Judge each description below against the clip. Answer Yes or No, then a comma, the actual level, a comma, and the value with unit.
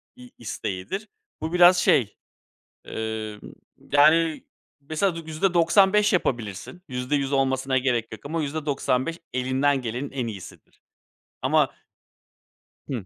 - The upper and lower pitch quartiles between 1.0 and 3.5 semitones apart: No, average, 5.0 semitones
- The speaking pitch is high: No, medium, 140 Hz